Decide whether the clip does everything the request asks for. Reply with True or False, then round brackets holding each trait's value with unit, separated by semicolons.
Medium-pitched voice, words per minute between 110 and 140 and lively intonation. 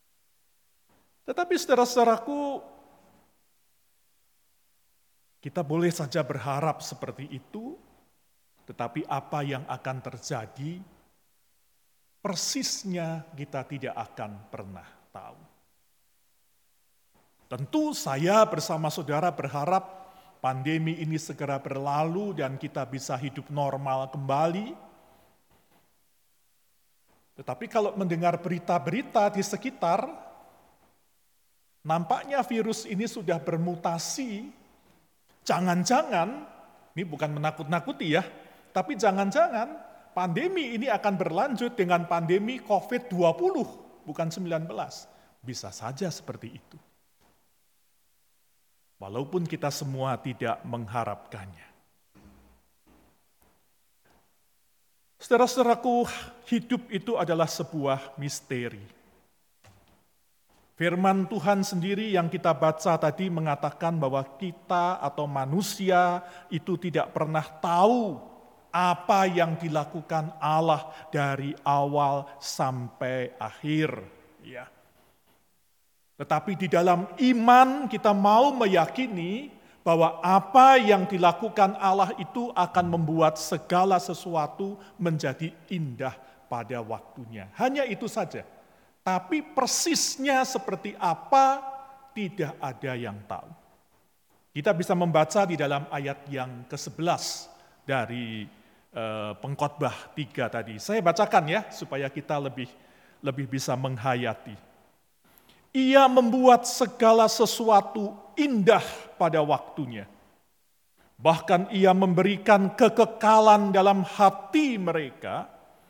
False (170 Hz; 85 wpm; 6.5 semitones)